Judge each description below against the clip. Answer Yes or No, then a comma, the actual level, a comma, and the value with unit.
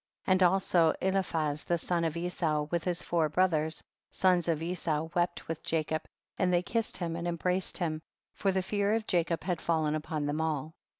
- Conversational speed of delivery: Yes, average, 190 wpm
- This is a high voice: No, medium, 170 Hz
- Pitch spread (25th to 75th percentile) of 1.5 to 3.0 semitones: Yes, narrow, 2.4 semitones